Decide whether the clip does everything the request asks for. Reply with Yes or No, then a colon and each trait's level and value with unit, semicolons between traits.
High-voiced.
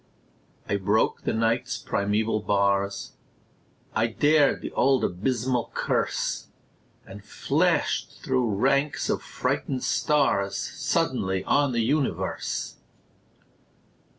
No: low, 115 Hz